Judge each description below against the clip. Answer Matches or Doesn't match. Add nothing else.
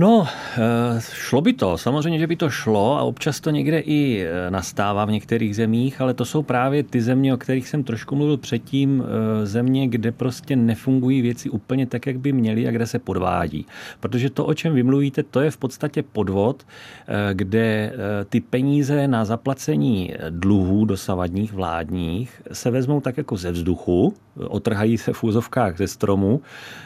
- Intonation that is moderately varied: Matches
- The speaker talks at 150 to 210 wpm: Matches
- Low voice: Matches